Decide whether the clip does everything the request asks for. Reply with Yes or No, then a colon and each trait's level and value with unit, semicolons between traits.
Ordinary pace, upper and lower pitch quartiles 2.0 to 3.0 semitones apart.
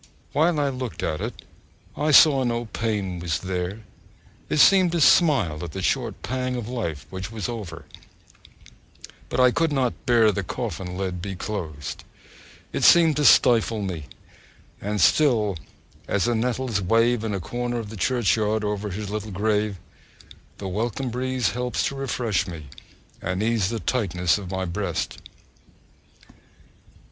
No: average, 155 wpm; average, 4.8 semitones